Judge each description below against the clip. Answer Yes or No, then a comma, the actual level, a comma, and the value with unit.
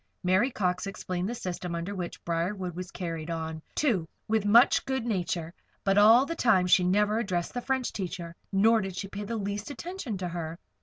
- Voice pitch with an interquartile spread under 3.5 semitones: No, average, 4.0 semitones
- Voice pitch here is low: No, high, 195 Hz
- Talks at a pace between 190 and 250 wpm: Yes, average, 195 wpm